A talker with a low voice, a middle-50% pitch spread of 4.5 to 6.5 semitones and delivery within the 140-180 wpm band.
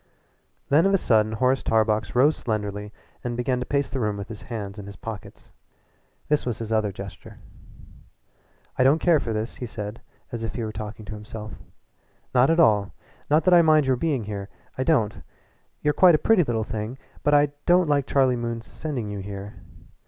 No: low, 115 Hz; average, 5.0 semitones; average, 195 wpm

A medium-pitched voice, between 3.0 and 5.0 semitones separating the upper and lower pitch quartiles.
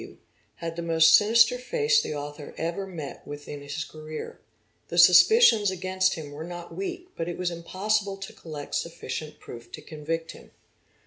Yes: medium, 170 Hz; average, 4.2 semitones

